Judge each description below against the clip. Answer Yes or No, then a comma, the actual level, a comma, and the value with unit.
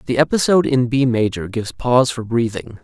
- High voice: No, low, 125 Hz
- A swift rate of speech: No, average, 190 wpm